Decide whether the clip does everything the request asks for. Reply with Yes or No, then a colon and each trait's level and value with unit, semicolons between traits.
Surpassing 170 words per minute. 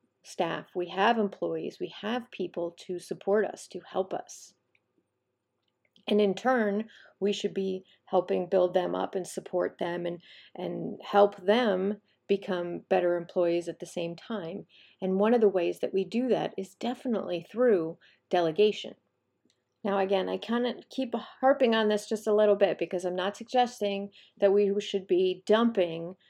No: average, 165 wpm